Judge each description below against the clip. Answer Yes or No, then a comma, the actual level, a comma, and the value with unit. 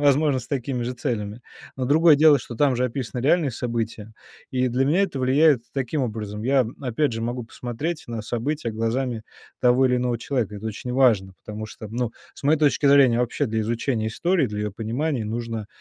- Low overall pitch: Yes, low, 125 Hz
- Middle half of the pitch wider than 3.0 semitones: Yes, average, 3.7 semitones